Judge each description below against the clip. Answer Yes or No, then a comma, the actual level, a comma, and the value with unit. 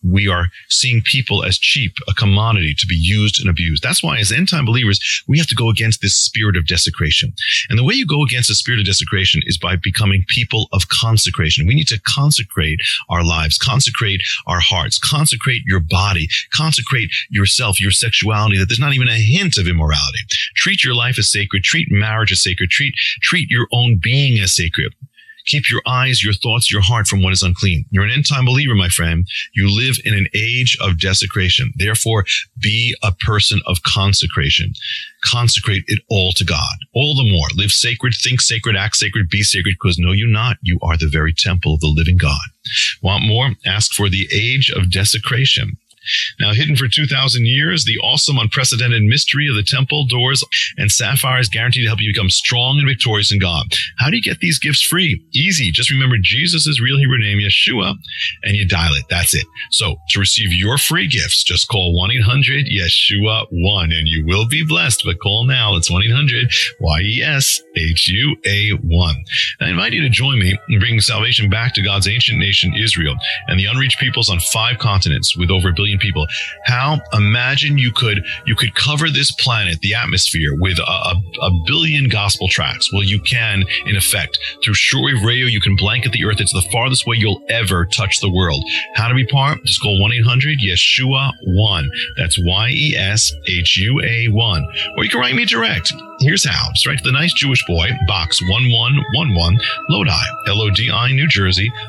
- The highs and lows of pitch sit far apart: No, average, 5.0 semitones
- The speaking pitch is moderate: No, low, 110 Hz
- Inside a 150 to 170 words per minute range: No, average, 200 wpm